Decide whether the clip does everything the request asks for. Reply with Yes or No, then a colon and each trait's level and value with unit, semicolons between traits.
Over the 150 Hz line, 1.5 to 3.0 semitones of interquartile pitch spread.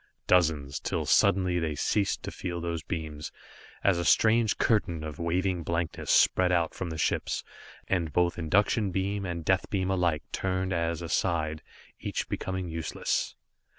No: very low, 85 Hz; narrow, 2.5 semitones